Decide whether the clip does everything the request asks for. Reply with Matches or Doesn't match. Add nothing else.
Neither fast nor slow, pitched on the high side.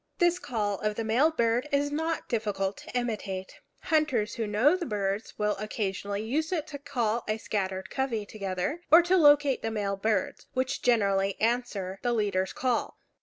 Matches